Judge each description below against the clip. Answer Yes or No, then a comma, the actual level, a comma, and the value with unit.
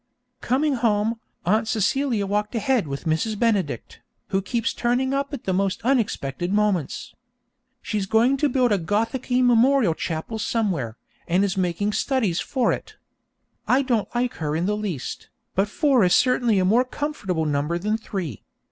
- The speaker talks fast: No, average, 160 wpm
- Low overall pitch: No, high, 210 Hz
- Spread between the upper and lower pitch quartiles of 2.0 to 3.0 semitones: No, average, 5.2 semitones